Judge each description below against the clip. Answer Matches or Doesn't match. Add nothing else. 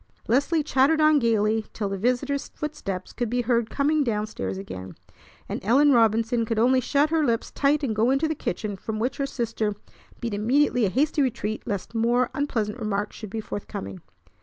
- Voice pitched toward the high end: Matches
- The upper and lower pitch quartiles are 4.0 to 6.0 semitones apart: Matches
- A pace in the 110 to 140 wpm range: Doesn't match